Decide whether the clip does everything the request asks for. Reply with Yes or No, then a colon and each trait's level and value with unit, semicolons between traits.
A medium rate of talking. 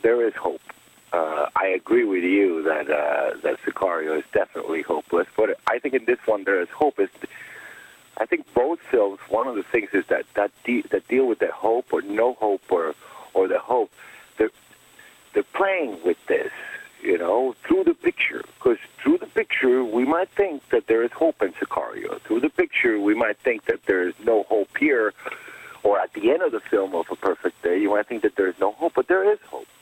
No: fast, 215 wpm